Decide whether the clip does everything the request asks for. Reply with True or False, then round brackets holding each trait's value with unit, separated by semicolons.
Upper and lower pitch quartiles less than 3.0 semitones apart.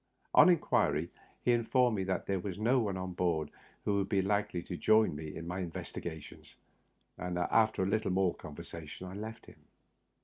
False (3.8 semitones)